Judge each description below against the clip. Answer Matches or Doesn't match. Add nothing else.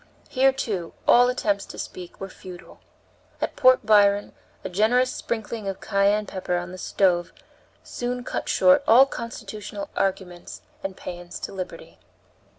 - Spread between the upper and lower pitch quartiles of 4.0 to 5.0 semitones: Matches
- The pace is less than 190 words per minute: Matches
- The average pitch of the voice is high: Matches